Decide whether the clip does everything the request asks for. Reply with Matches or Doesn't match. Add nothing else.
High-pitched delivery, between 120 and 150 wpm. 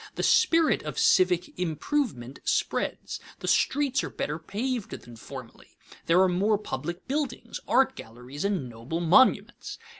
Doesn't match